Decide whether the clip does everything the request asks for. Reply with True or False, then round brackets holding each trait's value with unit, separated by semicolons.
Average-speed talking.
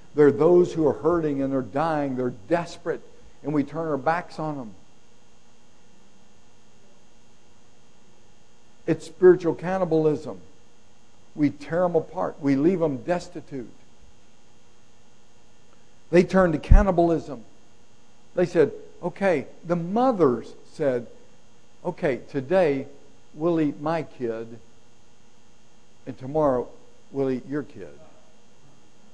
False (105 wpm)